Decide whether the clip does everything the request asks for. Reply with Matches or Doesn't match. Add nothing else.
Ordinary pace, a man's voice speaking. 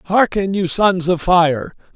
Matches